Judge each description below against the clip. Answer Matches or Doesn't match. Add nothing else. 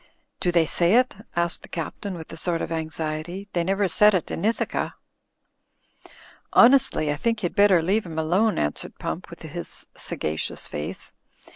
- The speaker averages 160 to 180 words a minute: Matches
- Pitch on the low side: Doesn't match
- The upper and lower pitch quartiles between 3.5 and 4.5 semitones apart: Matches